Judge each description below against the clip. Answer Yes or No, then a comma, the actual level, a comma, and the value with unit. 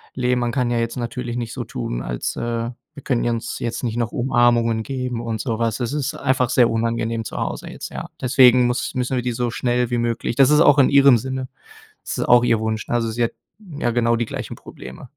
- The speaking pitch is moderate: No, low, 120 Hz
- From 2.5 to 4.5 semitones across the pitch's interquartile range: No, narrow, 1.6 semitones